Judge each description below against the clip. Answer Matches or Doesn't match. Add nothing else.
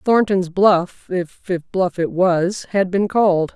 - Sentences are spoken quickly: Doesn't match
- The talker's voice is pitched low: Doesn't match